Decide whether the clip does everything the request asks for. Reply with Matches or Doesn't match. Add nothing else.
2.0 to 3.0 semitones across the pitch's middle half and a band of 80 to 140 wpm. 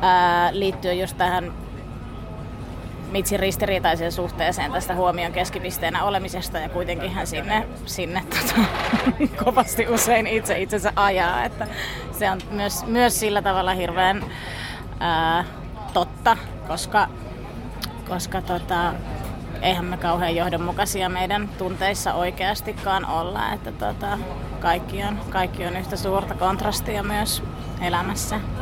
Matches